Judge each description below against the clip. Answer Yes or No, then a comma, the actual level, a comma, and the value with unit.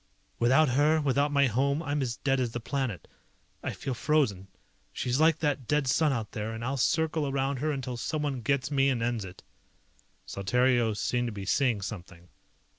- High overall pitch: No, low, 130 Hz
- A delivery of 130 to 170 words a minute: No, average, 185 wpm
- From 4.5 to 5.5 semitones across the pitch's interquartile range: No, average, 3.7 semitones